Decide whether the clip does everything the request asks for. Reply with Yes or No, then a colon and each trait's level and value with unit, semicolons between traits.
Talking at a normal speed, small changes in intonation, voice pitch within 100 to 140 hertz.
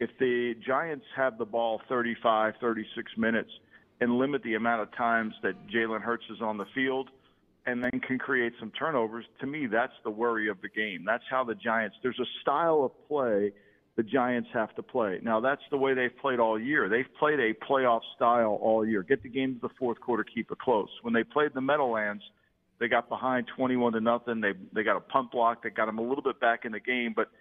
No: fast, 225 wpm; narrow, 2.2 semitones; low, 115 Hz